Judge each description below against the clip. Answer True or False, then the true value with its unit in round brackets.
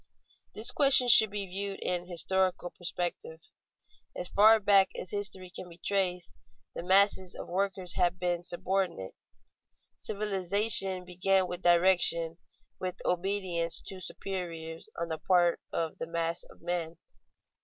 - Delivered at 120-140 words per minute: True (135 wpm)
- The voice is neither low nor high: True (180 Hz)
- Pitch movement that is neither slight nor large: False (2.1 semitones)